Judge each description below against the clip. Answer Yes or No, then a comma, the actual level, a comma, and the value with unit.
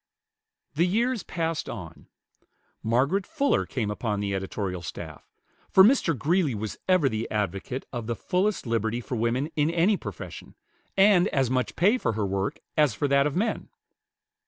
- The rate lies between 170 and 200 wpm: No, average, 160 wpm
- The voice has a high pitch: No, low, 135 Hz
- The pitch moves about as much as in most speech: No, wide, 8.8 semitones